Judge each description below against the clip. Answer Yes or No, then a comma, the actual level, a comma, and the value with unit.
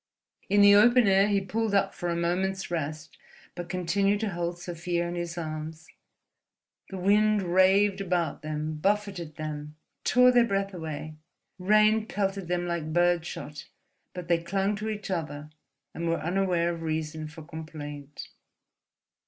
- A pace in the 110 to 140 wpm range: No, average, 150 wpm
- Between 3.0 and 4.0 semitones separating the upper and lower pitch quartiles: Yes, average, 3.6 semitones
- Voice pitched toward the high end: No, medium, 175 Hz